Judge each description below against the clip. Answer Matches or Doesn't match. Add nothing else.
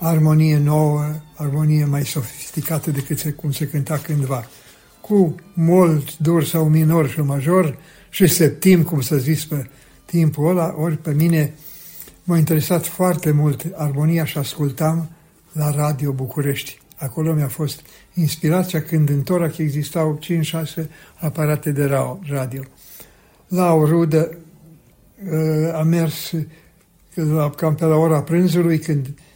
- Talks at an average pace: Matches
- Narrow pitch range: Matches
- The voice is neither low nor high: Matches